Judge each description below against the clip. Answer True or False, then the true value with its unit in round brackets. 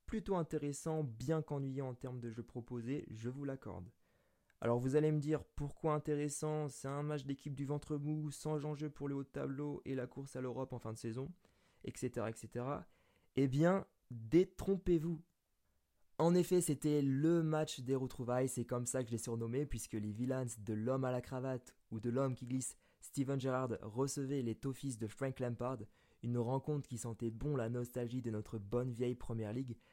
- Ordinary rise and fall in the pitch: True (3.7 semitones)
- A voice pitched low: True (130 Hz)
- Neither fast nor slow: True (195 wpm)